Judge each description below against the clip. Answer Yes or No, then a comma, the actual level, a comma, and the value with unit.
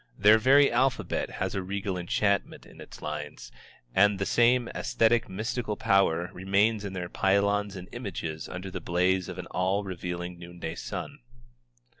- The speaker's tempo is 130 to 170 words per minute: Yes, average, 155 wpm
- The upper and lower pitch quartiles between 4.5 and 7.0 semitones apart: No, average, 2.8 semitones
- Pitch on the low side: Yes, very low, 95 Hz